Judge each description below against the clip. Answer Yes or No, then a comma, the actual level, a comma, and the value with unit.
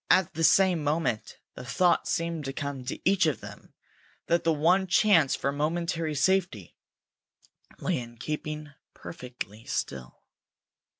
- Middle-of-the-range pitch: Yes, medium, 155 Hz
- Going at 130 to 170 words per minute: Yes, slow, 135 wpm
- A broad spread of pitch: No, average, 4.0 semitones